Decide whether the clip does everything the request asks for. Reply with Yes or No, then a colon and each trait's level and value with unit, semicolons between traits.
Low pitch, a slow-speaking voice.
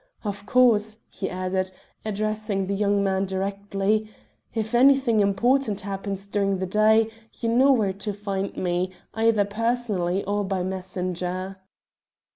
No: high, 200 Hz; slow, 130 wpm